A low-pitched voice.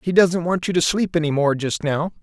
No: medium, 165 Hz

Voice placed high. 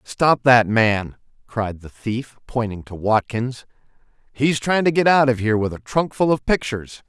No: low, 125 Hz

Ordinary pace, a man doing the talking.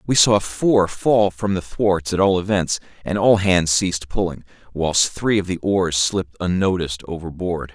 Yes: average, 180 wpm; male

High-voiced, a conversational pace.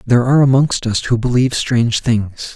No: low, 120 Hz; average, 190 wpm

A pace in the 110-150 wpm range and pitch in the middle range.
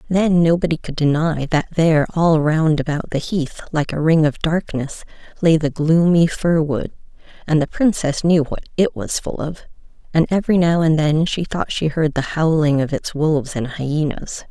No: average, 190 wpm; medium, 155 Hz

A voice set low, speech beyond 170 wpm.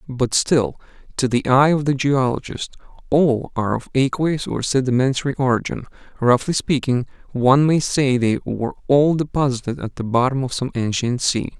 No: low, 130 Hz; average, 160 wpm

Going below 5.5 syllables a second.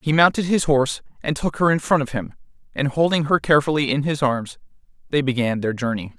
No: 6.1 syllables/s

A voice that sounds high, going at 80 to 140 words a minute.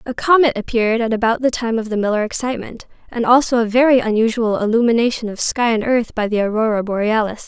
No: high, 230 Hz; average, 200 wpm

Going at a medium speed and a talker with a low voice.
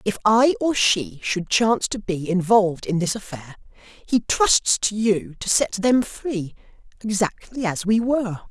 No: average, 170 wpm; high, 205 Hz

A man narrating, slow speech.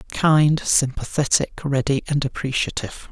Yes: male; slow, 95 wpm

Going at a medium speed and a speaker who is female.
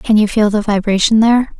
No: fast, 225 wpm; female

